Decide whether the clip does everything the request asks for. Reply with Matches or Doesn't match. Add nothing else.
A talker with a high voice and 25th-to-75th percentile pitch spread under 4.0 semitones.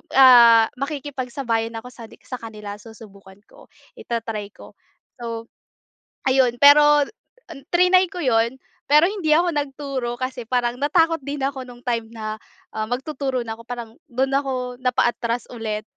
Matches